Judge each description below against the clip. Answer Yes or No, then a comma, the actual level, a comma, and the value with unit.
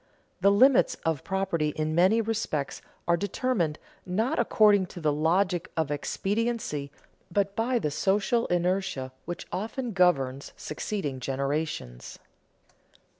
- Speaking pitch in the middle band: Yes, medium, 180 Hz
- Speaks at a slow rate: Yes, slow, 120 wpm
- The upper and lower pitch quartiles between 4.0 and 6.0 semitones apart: Yes, wide, 5.5 semitones